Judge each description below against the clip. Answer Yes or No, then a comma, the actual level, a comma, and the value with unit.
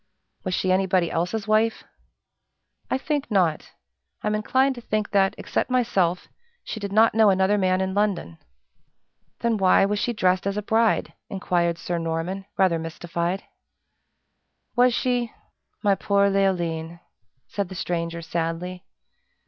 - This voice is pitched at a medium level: No, high, 195 Hz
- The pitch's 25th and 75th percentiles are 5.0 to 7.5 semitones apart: No, average, 3.6 semitones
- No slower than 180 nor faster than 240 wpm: No, average, 140 wpm